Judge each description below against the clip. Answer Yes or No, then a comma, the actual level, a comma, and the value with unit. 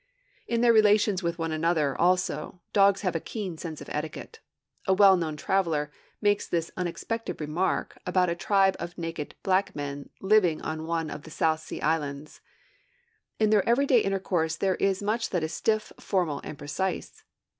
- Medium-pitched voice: Yes, medium, 180 Hz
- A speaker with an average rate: Yes, average, 170 wpm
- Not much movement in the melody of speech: No, average, 3.9 semitones